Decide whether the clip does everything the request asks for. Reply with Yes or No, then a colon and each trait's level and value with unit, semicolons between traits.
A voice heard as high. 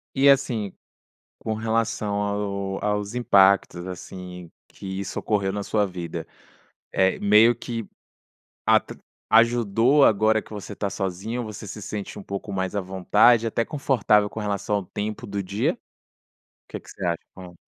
No: low, 105 Hz